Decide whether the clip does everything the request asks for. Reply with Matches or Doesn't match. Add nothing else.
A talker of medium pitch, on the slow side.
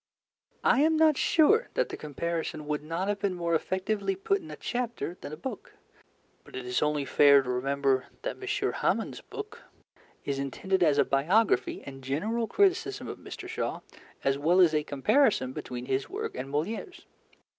Doesn't match